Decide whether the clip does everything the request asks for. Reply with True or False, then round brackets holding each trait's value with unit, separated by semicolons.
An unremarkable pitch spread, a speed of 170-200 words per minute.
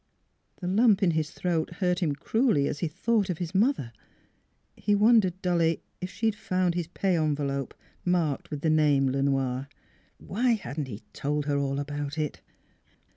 True (4.8 semitones; 175 wpm)